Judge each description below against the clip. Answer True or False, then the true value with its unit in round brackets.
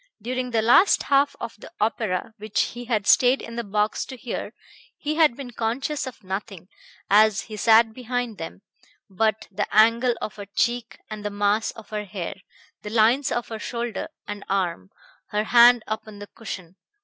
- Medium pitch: False (220 Hz)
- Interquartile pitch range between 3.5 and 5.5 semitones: False (2.7 semitones)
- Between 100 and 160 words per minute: False (180 wpm)